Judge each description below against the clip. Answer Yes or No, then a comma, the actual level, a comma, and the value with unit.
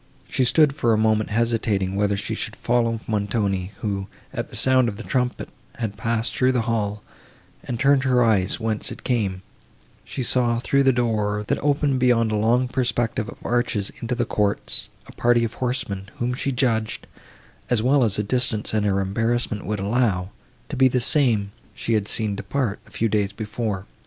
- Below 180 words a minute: No, average, 185 wpm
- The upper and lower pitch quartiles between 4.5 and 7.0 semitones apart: No, average, 3.1 semitones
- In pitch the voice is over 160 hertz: No, low, 115 Hz